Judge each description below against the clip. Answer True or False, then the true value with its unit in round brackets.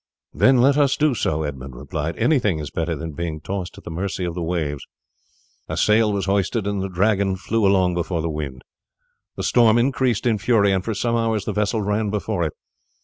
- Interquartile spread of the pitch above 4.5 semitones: True (5.1 semitones)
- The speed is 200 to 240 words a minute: True (205 wpm)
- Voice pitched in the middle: False (100 Hz)